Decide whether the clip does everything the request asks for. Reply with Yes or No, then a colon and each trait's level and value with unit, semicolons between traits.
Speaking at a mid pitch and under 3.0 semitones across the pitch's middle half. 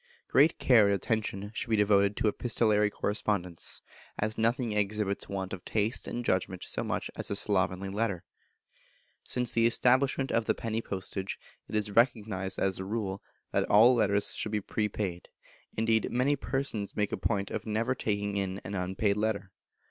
No: low, 105 Hz; narrow, 2.5 semitones